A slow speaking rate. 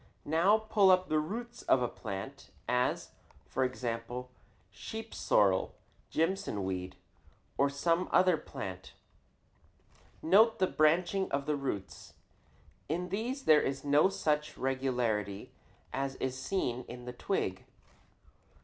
Yes: slow, 120 wpm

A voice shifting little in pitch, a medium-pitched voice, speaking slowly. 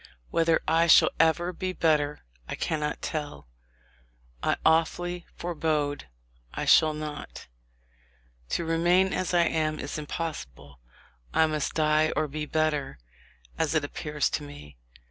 Yes: narrow, 1.8 semitones; medium, 155 Hz; slow, 130 wpm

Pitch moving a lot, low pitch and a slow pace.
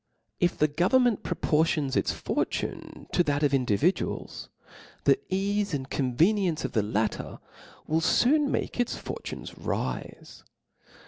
No: wide, 6.6 semitones; medium, 160 Hz; slow, 130 wpm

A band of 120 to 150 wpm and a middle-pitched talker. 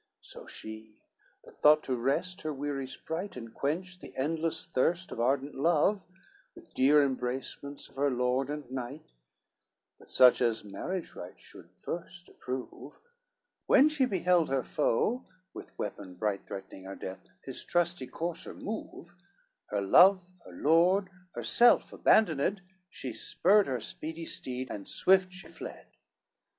Yes: average, 145 wpm; medium, 150 Hz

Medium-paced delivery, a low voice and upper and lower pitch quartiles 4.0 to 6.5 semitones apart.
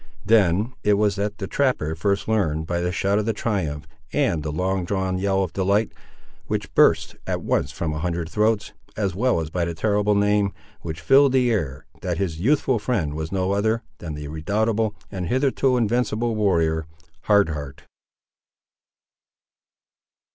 Yes: average, 160 wpm; low, 100 Hz; average, 4.7 semitones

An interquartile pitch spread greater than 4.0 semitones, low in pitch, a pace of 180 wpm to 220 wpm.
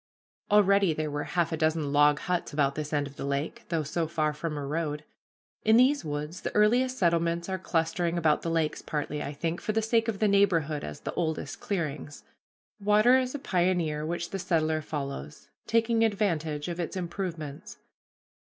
No: average, 4.7 semitones; medium, 165 Hz; average, 185 wpm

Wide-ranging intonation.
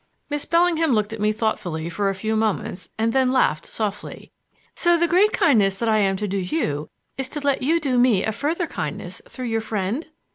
Yes: wide, 6.3 semitones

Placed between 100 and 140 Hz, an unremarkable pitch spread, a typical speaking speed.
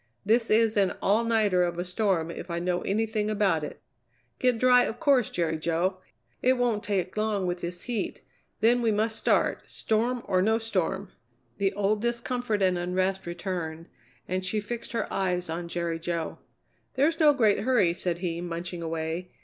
No: high, 195 Hz; average, 4.2 semitones; average, 175 wpm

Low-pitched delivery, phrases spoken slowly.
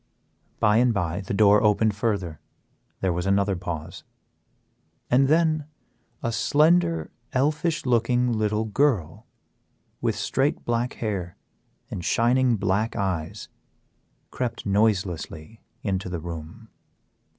Yes: low, 105 Hz; slow, 110 wpm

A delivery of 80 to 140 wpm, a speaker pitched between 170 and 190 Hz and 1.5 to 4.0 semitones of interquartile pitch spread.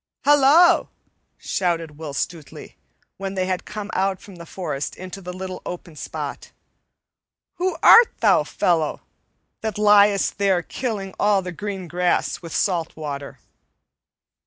Yes: slow, 135 wpm; medium, 185 Hz; average, 3.3 semitones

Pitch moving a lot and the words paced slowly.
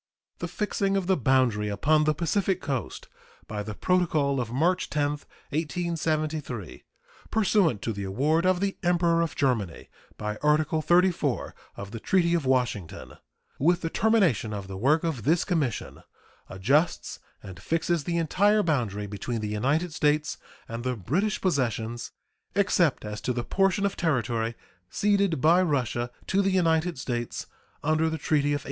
No: wide, 6.6 semitones; average, 155 wpm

